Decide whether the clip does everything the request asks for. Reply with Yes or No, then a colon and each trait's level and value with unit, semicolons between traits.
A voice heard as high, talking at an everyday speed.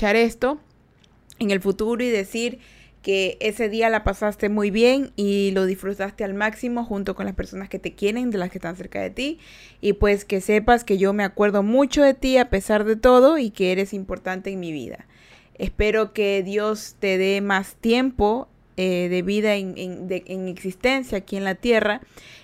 No: high, 205 Hz; fast, 195 wpm